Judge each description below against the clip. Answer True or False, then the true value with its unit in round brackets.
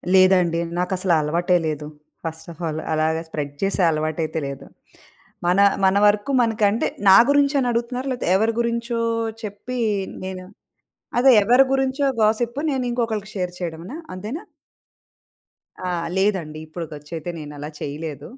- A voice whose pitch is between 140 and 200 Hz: True (190 Hz)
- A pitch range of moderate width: False (6.5 semitones)